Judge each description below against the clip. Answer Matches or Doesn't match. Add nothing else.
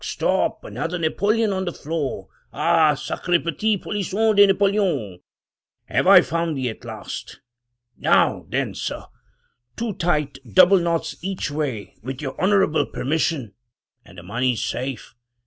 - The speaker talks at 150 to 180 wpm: Doesn't match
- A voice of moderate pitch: Matches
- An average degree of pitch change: Doesn't match